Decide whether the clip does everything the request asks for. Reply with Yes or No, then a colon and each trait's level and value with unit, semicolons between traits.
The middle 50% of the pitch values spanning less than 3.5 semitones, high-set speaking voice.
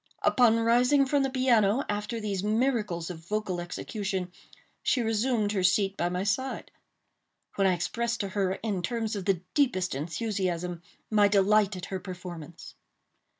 No: average, 3.9 semitones; high, 205 Hz